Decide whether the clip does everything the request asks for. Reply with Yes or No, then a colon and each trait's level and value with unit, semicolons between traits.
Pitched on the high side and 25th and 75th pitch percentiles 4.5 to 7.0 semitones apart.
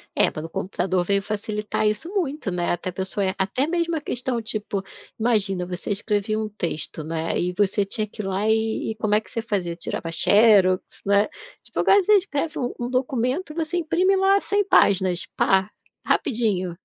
Yes: high, 210 Hz; average, 5.2 semitones